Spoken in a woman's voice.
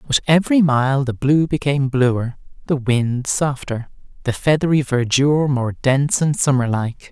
No: male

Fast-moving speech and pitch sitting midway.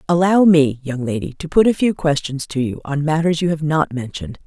Yes: fast, 230 wpm; medium, 155 Hz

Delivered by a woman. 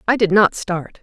Yes: female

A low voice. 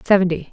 No: medium, 175 Hz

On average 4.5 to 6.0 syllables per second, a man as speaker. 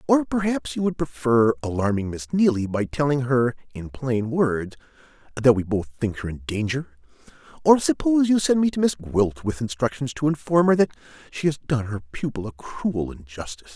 Yes: 5.1 syllables/s; male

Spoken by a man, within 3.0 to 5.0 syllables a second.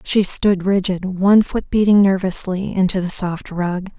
No: female; 4.4 syllables/s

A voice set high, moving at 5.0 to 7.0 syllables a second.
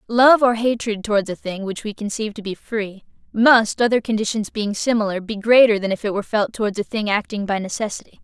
Yes: high, 215 Hz; 5.9 syllables/s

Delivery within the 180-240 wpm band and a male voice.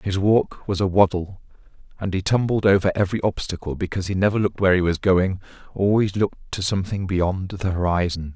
Yes: average, 185 wpm; male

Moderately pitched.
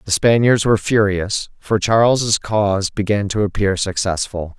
No: low, 105 Hz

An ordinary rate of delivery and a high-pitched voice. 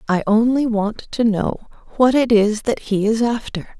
Yes: average, 190 wpm; high, 220 Hz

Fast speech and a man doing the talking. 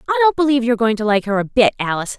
No: fast, 330 wpm; female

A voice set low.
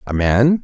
Yes: low, 120 Hz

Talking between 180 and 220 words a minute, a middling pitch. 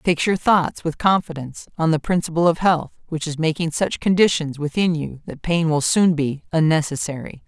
Yes: average, 185 wpm; medium, 160 Hz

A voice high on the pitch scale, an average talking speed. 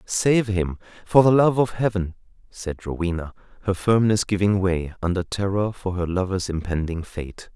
No: very low, 95 Hz; average, 160 wpm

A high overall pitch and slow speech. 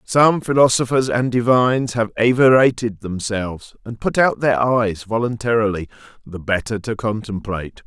No: low, 115 Hz; slow, 130 wpm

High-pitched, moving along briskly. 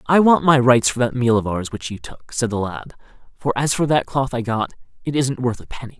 No: low, 125 Hz; fast, 270 wpm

